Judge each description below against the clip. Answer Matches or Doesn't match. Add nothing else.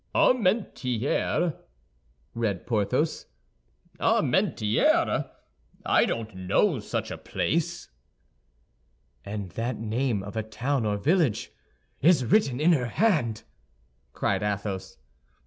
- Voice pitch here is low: Matches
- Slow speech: Matches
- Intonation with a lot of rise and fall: Matches